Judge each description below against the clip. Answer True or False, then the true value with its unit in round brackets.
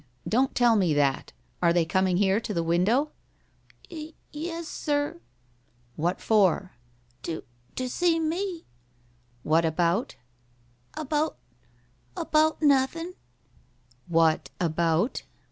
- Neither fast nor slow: False (110 wpm)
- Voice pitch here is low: False (220 Hz)